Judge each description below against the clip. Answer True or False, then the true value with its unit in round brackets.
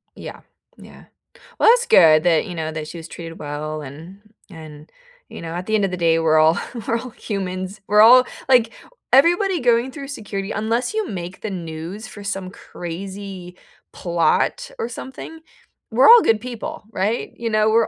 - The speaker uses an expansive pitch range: True (5.8 semitones)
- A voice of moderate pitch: False (195 Hz)